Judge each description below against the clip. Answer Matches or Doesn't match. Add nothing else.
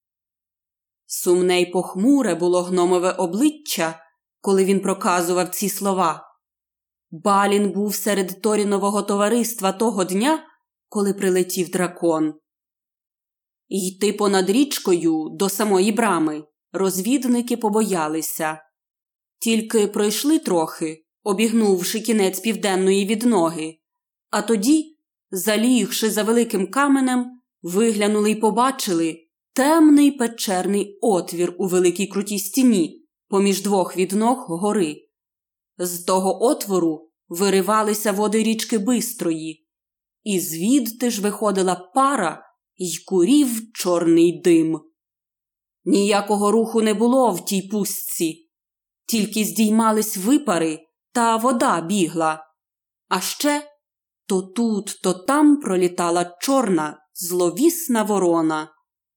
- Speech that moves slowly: Matches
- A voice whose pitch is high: Matches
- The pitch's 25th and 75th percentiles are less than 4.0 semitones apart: Doesn't match